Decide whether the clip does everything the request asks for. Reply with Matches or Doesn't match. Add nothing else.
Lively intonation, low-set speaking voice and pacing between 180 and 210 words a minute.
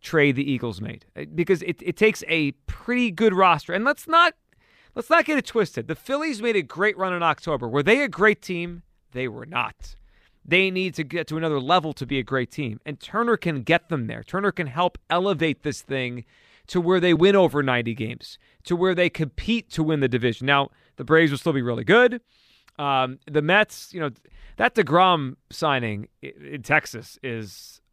Doesn't match